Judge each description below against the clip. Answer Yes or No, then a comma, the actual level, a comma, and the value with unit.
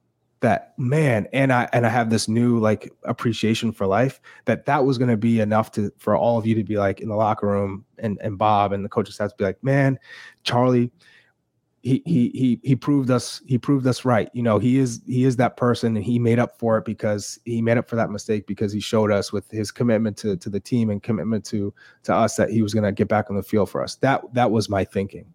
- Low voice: Yes, low, 110 Hz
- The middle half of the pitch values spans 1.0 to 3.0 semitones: Yes, average, 2.7 semitones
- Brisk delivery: Yes, fast, 255 wpm